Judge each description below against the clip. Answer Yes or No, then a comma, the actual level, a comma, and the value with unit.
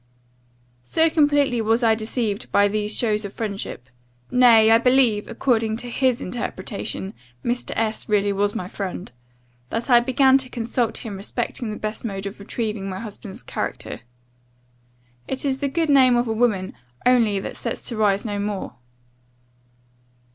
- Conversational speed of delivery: Yes, average, 155 wpm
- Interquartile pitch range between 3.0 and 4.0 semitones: Yes, average, 3.3 semitones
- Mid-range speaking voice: No, high, 225 Hz